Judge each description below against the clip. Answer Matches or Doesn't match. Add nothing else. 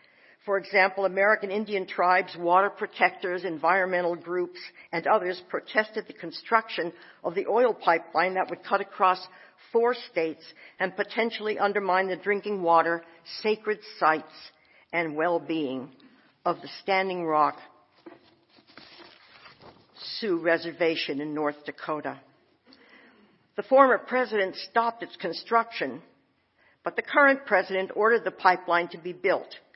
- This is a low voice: Doesn't match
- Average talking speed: Doesn't match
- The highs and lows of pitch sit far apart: Doesn't match